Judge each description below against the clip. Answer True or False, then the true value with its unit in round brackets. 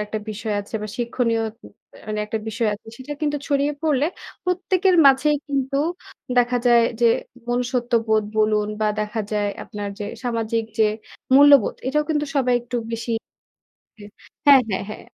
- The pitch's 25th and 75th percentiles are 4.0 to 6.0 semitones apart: True (4.3 semitones)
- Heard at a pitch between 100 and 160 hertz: False (240 Hz)